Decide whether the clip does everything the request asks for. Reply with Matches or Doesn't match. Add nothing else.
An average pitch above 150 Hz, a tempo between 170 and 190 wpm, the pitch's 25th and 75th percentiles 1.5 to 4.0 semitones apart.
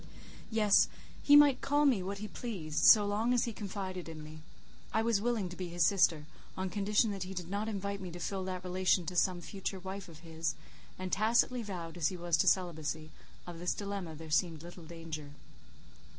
Doesn't match